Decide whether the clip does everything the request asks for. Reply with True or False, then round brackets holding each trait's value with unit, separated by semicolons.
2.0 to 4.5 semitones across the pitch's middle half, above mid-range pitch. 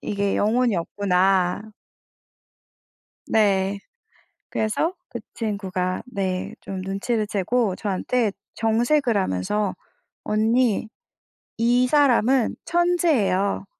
True (4.0 semitones; 210 Hz)